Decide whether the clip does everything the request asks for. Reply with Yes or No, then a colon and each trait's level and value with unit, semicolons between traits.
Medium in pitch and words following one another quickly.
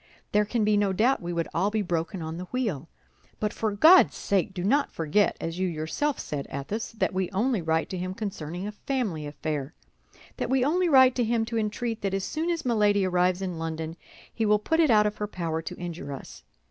No: high, 200 Hz; fast, 225 wpm